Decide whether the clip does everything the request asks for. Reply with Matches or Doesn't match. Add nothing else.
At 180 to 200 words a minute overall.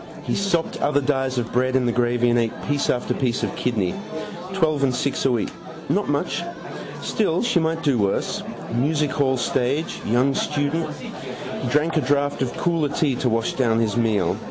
Matches